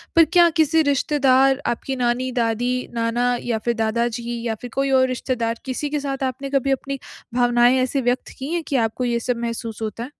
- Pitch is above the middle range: Yes, very high, 250 Hz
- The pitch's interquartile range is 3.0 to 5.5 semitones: No, narrow, 2.5 semitones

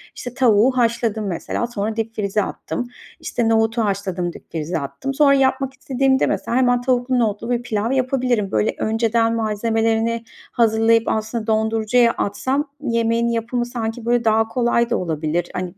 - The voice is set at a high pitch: Yes, high, 230 Hz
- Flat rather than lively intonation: Yes, narrow, 2.2 semitones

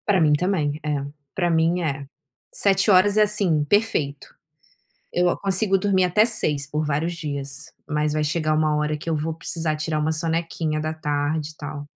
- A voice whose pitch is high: No, medium, 155 Hz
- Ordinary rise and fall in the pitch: Yes, average, 3.0 semitones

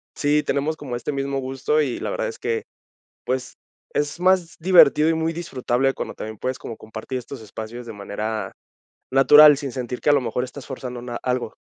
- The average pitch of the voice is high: No, low, 135 Hz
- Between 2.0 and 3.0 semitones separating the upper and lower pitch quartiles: No, average, 3.6 semitones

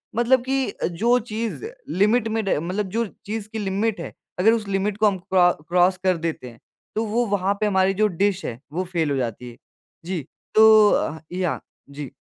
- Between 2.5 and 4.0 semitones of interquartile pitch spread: Yes, average, 3.5 semitones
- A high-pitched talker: Yes, high, 195 Hz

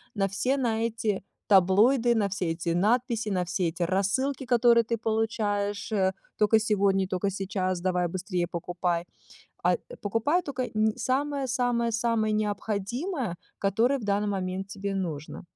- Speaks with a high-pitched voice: Yes, high, 205 Hz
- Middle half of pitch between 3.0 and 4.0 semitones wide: Yes, average, 3.7 semitones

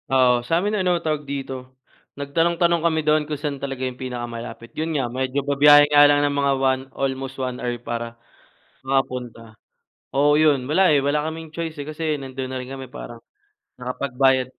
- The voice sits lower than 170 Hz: Yes, low, 135 Hz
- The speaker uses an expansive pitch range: No, average, 2.8 semitones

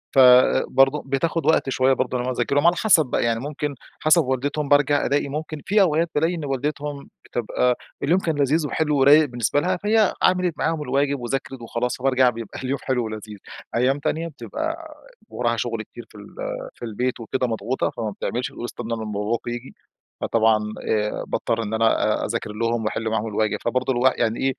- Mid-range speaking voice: No, low, 130 Hz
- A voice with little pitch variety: No, average, 4.2 semitones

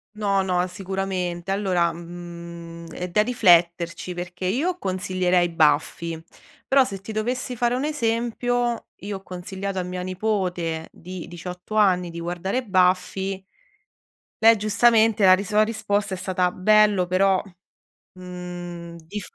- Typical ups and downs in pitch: Yes, average, 3.1 semitones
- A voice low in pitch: No, medium, 185 Hz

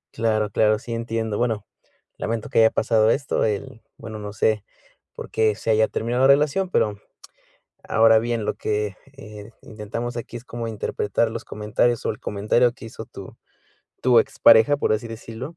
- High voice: No, low, 115 Hz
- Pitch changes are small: Yes, narrow, 1.7 semitones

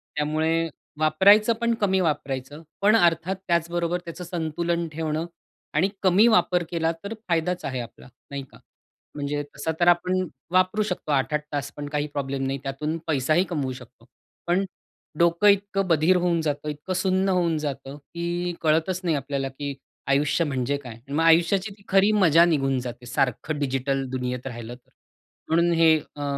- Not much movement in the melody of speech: No, average, 3.9 semitones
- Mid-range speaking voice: Yes, medium, 160 Hz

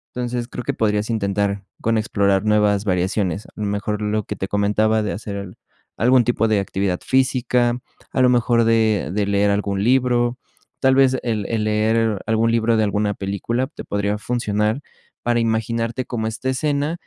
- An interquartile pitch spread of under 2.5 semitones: No, average, 2.8 semitones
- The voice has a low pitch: Yes, low, 110 Hz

